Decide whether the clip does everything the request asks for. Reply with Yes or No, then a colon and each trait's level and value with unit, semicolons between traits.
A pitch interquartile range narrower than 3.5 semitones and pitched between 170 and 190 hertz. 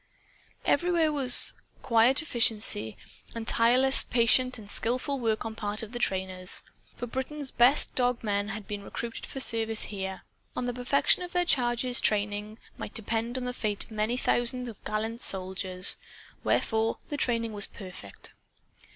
No: average, 3.1 semitones; high, 230 Hz